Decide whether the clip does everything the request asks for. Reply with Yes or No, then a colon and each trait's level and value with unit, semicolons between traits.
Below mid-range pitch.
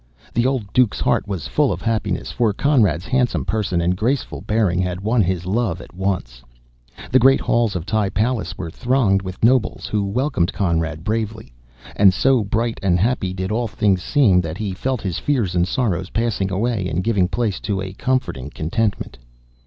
Yes: low, 100 Hz